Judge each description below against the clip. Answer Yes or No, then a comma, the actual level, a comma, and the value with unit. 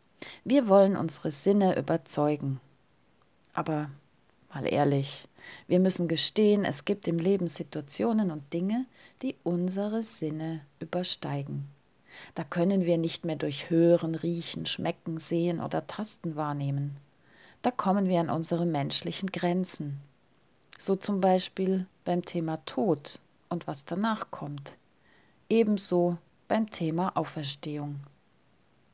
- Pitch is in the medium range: Yes, medium, 170 Hz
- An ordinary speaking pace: No, slow, 115 wpm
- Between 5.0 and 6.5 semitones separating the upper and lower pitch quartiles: No, average, 4.2 semitones